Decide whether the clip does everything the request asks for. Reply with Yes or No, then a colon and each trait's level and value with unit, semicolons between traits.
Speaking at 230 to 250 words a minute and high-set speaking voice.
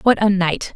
Yes: fast, 240 wpm; high, 195 Hz